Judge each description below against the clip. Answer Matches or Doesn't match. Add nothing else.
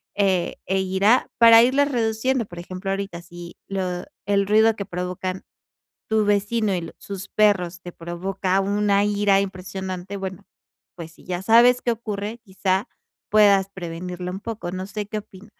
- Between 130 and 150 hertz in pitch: Doesn't match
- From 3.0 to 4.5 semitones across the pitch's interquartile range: Doesn't match